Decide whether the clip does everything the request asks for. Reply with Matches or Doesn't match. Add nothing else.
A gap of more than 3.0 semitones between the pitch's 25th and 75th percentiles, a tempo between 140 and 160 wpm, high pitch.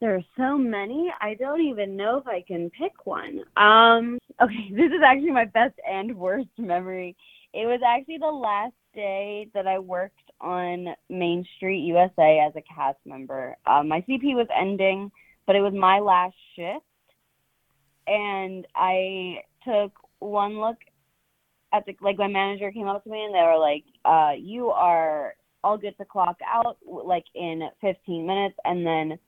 Doesn't match